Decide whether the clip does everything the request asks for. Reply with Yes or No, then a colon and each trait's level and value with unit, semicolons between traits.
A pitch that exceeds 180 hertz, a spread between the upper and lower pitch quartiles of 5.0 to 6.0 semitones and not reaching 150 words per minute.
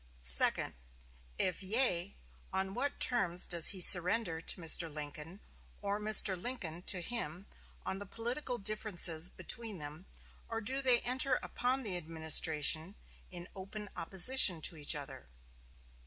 Yes: high, 190 Hz; wide, 5.6 semitones; slow, 135 wpm